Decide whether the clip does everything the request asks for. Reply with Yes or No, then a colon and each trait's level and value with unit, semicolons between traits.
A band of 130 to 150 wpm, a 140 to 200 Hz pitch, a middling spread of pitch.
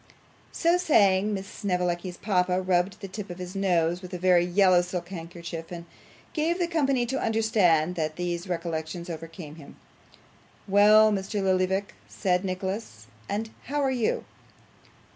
Yes: average, 145 wpm; medium, 185 Hz; average, 3.1 semitones